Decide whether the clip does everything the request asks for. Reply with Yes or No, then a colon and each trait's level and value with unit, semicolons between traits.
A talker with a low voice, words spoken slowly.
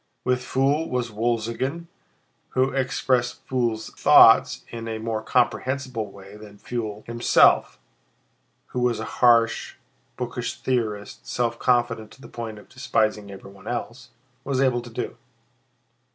Yes: low, 120 Hz; slow, 130 wpm